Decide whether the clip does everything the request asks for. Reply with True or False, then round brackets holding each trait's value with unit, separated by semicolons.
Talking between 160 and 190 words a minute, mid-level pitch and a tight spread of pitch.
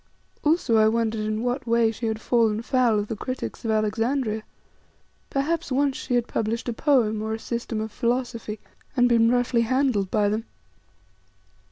False (170 wpm; 230 Hz; 2.3 semitones)